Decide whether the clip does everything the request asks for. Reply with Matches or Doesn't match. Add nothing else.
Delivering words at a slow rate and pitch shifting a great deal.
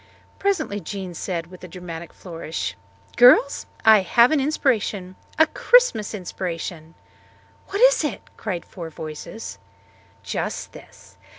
Matches